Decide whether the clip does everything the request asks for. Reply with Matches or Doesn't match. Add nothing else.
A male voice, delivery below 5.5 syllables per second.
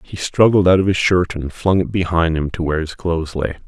Doesn't match